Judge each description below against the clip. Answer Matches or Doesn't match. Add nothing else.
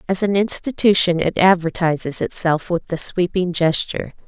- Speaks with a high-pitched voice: Doesn't match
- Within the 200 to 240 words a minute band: Doesn't match